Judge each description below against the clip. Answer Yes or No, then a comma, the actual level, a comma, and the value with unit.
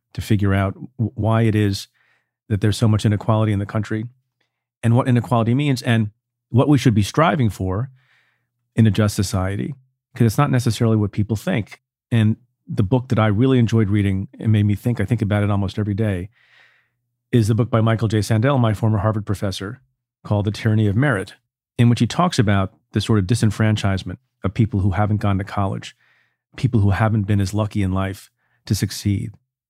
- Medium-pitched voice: No, low, 110 Hz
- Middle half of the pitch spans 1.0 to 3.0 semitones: Yes, average, 2.7 semitones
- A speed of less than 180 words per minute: No, average, 195 wpm